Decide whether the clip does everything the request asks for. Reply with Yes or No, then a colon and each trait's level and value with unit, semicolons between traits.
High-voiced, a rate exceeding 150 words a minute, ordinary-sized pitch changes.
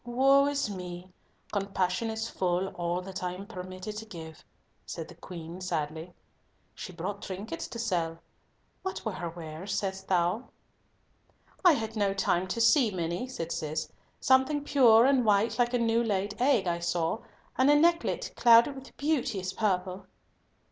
Yes: high, 195 Hz; average, 160 wpm; average, 4.8 semitones